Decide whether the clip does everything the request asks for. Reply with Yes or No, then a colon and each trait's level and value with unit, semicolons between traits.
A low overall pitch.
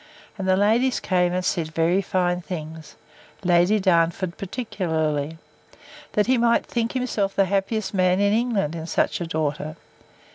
No: medium, 185 Hz